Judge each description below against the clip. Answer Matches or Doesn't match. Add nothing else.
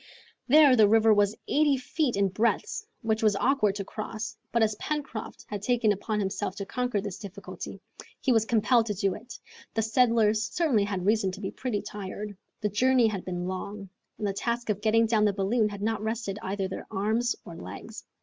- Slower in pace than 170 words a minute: Doesn't match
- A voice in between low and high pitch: Doesn't match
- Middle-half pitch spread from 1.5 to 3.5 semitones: Matches